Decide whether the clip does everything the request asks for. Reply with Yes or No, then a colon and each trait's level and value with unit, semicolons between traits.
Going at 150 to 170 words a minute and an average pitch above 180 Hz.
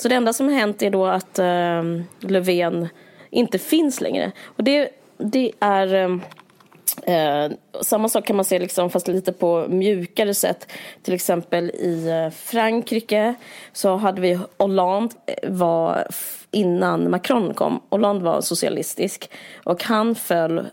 No: average, 140 wpm; high, 190 Hz